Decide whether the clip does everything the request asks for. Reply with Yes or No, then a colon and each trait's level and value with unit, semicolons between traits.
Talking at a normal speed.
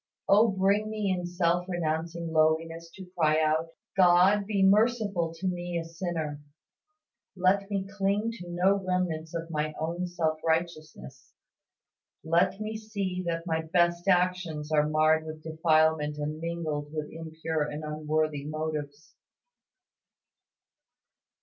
No: slow, 130 wpm